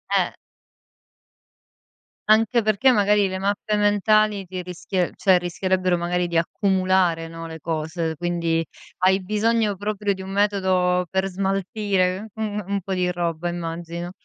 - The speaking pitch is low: No, medium, 185 Hz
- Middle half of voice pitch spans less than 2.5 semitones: No, average, 2.8 semitones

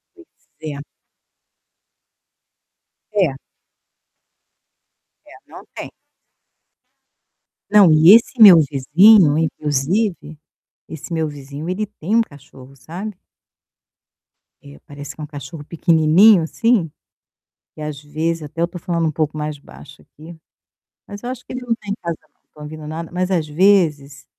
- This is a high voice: No, medium, 160 Hz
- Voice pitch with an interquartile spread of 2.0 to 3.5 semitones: No, average, 4.6 semitones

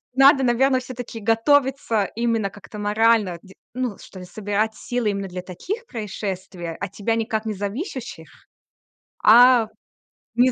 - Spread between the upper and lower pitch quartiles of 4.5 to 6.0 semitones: No, average, 3.8 semitones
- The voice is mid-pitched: No, high, 225 Hz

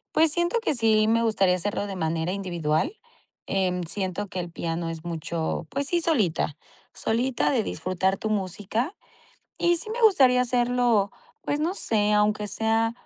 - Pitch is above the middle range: Yes, high, 210 Hz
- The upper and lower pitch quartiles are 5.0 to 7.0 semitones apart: Yes, wide, 5.5 semitones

